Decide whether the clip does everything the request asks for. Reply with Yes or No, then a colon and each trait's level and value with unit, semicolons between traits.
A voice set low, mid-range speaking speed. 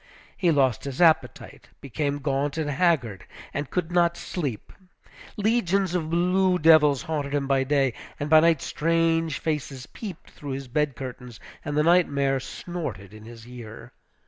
No: medium, 145 Hz; average, 160 wpm